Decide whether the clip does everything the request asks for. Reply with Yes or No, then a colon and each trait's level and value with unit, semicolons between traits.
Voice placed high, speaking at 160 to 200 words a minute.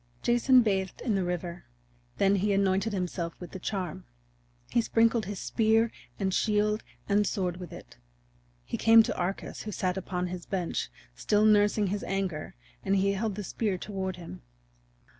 Yes: high, 195 Hz; average, 165 wpm